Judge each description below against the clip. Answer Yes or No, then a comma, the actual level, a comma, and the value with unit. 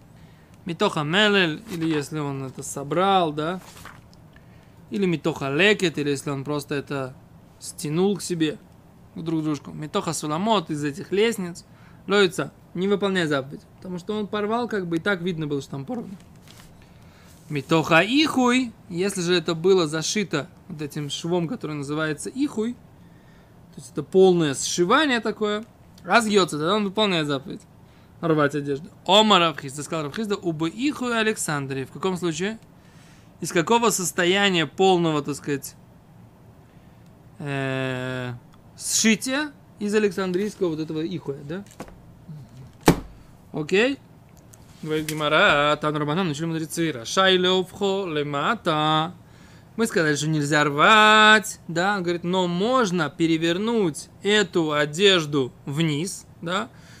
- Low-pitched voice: No, medium, 170 Hz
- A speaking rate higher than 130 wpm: No, average, 120 wpm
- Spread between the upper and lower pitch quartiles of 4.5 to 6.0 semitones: Yes, average, 5.0 semitones